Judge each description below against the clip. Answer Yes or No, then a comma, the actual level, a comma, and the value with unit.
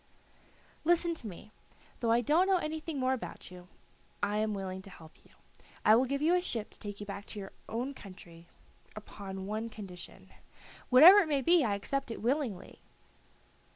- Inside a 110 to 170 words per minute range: No, average, 185 wpm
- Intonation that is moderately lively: No, wide, 6.5 semitones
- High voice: Yes, high, 225 Hz